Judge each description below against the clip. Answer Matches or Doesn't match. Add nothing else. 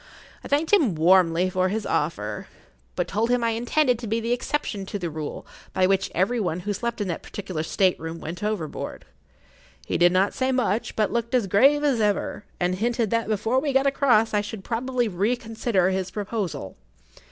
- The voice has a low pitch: Doesn't match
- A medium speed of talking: Matches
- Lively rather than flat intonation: Doesn't match